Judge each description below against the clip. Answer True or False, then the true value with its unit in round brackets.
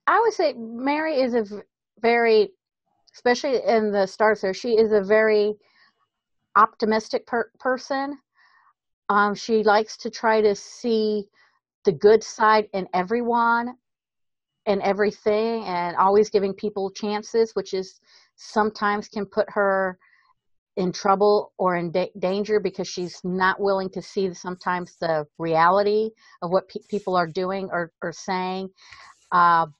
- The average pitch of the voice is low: False (205 Hz)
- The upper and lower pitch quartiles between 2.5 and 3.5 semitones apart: True (3.1 semitones)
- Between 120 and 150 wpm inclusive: True (140 wpm)